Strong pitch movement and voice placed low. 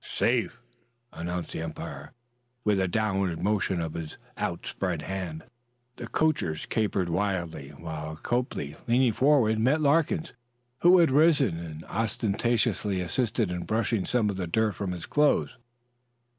Yes: wide, 6.0 semitones; low, 100 Hz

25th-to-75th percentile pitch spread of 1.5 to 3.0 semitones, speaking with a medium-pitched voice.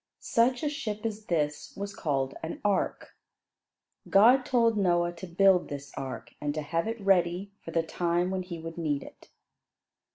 No: average, 4.2 semitones; medium, 175 Hz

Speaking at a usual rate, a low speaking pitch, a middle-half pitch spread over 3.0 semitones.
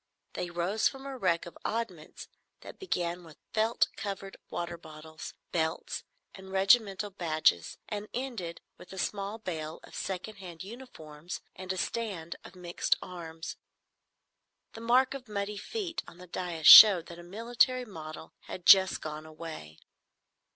No: average, 150 wpm; medium, 185 Hz; average, 4.5 semitones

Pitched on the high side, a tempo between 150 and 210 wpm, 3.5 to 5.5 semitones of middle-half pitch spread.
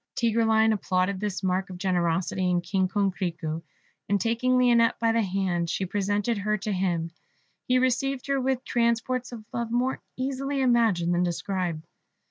Yes: high, 205 Hz; average, 155 wpm; average, 4.6 semitones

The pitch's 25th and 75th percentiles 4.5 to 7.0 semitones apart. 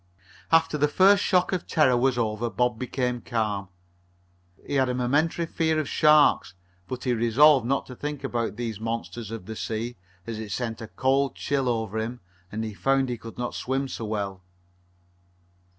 No: average, 3.8 semitones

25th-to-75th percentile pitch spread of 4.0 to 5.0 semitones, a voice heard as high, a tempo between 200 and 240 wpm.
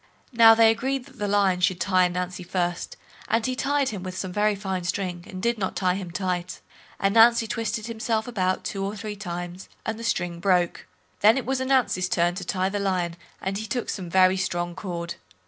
No: average, 3.6 semitones; high, 195 Hz; fast, 205 wpm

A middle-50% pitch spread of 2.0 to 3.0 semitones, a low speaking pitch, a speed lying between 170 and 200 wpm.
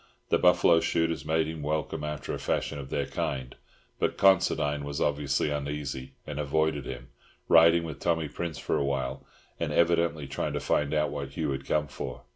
Yes: narrow, 2.5 semitones; very low, 75 Hz; average, 185 wpm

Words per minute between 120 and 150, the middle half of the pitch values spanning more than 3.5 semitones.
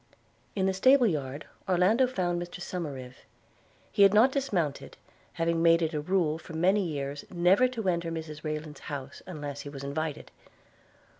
No: average, 160 wpm; average, 4.2 semitones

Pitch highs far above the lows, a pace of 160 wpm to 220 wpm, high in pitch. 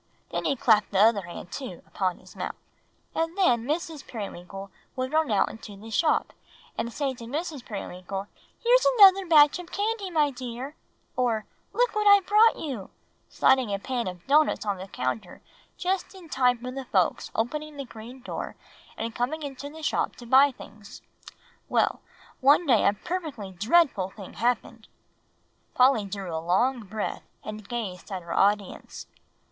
Yes: wide, 6.8 semitones; average, 165 wpm; high, 245 Hz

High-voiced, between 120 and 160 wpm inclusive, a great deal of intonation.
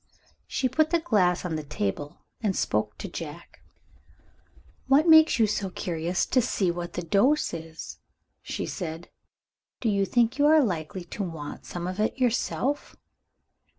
Yes: high, 195 Hz; average, 155 wpm; wide, 6.9 semitones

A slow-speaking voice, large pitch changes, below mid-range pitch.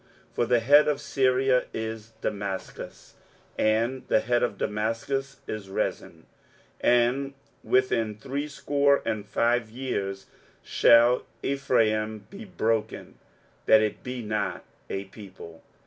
No: slow, 115 wpm; average, 3.7 semitones; low, 115 Hz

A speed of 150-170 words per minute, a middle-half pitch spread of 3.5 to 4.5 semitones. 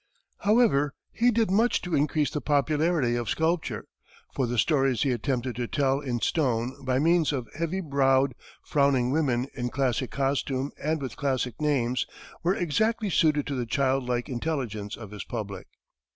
Yes: average, 165 wpm; average, 4.0 semitones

